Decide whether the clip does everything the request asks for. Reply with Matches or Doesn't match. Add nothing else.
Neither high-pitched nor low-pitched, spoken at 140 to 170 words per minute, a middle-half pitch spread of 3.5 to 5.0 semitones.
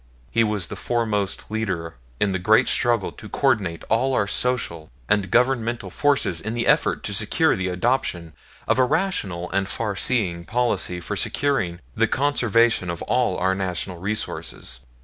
Doesn't match